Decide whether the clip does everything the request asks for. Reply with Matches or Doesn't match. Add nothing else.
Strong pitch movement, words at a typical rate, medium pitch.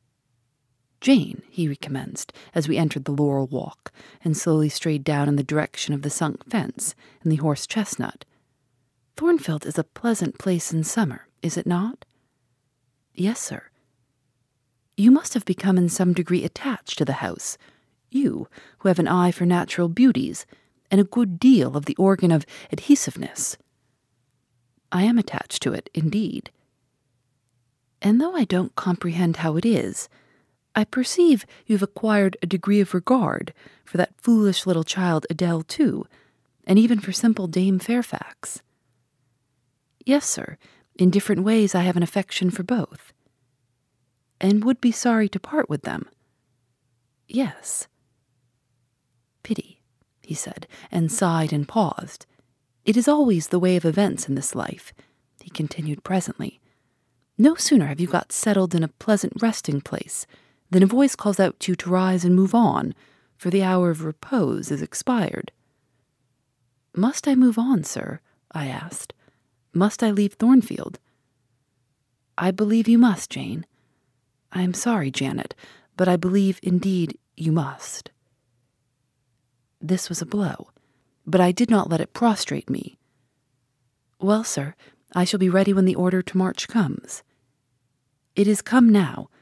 Matches